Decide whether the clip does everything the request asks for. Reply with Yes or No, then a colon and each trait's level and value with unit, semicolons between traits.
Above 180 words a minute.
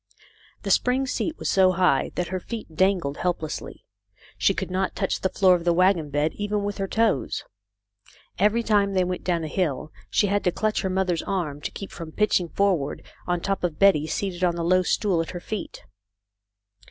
Yes: average, 200 wpm